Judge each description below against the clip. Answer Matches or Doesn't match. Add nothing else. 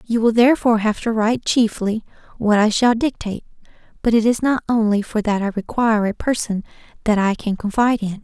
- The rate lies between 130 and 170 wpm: Doesn't match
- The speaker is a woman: Matches